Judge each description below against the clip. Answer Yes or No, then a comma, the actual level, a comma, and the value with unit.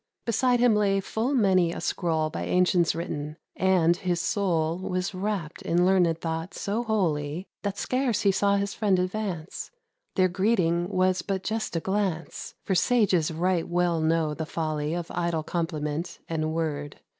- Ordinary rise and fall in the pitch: Yes, average, 3.4 semitones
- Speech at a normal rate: Yes, average, 160 wpm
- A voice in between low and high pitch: Yes, medium, 180 Hz